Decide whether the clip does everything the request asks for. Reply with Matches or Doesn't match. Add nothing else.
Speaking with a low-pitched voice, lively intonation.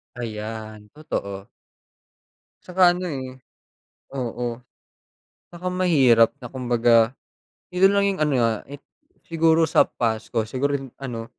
Matches